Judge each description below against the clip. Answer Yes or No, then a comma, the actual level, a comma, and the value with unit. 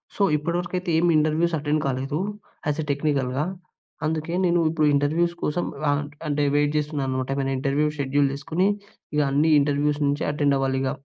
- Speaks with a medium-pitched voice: Yes, medium, 150 Hz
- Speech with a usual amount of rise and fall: No, narrow, 2.1 semitones